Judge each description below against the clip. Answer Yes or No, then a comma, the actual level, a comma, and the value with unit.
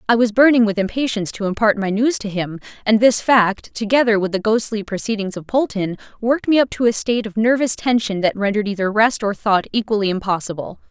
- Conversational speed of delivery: No, fast, 210 wpm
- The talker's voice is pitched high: Yes, high, 215 Hz